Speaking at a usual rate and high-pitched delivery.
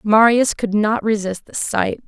Yes: average, 175 wpm; high, 215 Hz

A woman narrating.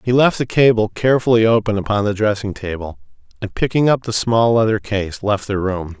No: male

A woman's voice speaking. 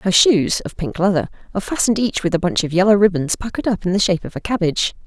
Yes: female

